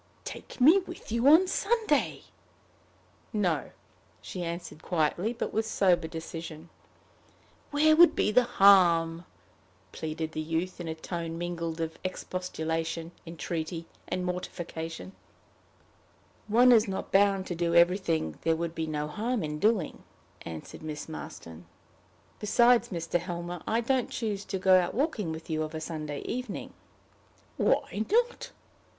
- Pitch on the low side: No, medium, 175 Hz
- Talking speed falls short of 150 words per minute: Yes, slow, 135 wpm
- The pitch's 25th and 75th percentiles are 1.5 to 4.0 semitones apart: No, average, 5.1 semitones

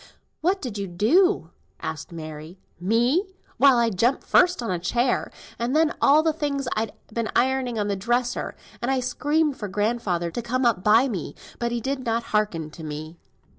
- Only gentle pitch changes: No, average, 5.2 semitones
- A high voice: Yes, high, 235 Hz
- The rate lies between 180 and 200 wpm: Yes, average, 190 wpm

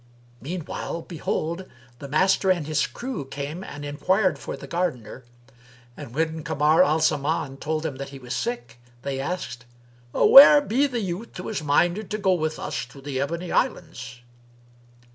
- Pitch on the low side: No, medium, 155 Hz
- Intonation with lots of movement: No, average, 4.8 semitones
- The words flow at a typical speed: Yes, average, 160 wpm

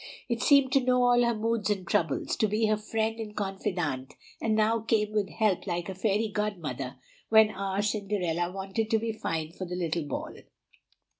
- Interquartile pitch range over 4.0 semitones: No, average, 3.6 semitones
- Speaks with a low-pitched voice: No, high, 210 Hz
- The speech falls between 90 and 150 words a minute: No, average, 190 wpm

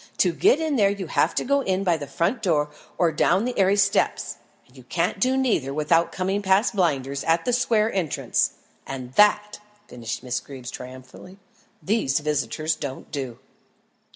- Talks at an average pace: Yes, average, 175 wpm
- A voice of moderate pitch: Yes, medium, 175 Hz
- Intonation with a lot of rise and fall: Yes, wide, 6.8 semitones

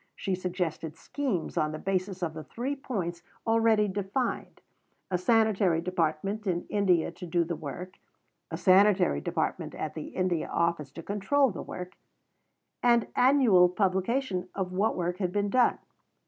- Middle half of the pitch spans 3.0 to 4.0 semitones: Yes, average, 3.7 semitones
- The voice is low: No, medium, 185 Hz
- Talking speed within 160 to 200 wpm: No, average, 150 wpm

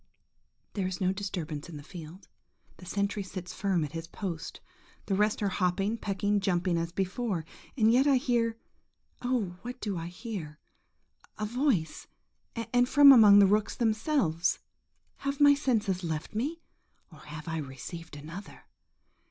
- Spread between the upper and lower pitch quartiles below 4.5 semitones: No, average, 5.2 semitones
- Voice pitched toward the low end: No, high, 195 Hz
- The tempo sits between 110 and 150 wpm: Yes, average, 145 wpm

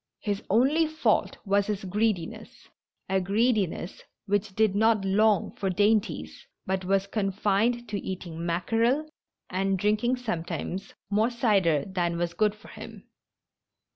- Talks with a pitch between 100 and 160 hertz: No, high, 200 Hz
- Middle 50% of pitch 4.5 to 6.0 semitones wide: No, average, 2.8 semitones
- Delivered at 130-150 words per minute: Yes, average, 140 wpm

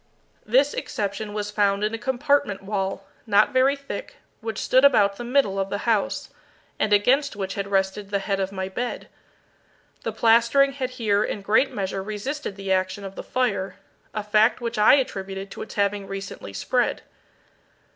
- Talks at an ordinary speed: Yes, average, 175 wpm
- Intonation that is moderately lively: Yes, average, 3.9 semitones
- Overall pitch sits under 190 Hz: No, high, 210 Hz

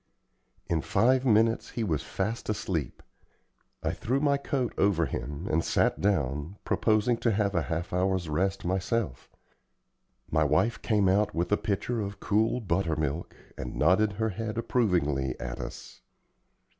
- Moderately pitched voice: No, very low, 95 Hz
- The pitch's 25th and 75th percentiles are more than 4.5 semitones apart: Yes, average, 5.2 semitones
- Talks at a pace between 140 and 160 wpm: Yes, average, 150 wpm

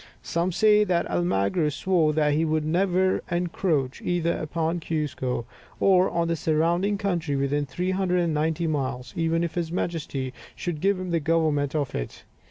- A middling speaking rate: Yes, average, 155 wpm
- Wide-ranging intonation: No, average, 3.1 semitones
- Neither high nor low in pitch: Yes, medium, 165 Hz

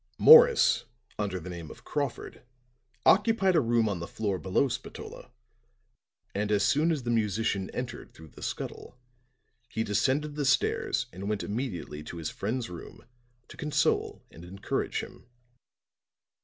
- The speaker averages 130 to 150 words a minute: Yes, average, 145 wpm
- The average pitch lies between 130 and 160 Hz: No, low, 110 Hz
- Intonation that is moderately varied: No, wide, 7.1 semitones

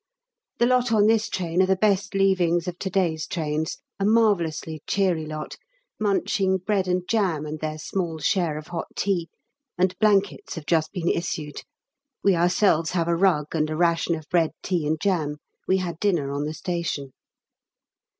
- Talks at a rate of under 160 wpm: No, average, 175 wpm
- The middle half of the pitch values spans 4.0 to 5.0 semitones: No, average, 3.6 semitones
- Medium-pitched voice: Yes, medium, 175 Hz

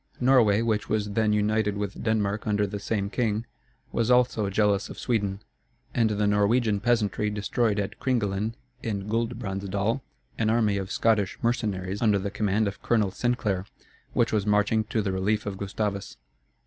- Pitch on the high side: No, low, 105 Hz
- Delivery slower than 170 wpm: Yes, average, 160 wpm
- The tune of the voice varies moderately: No, narrow, 2.0 semitones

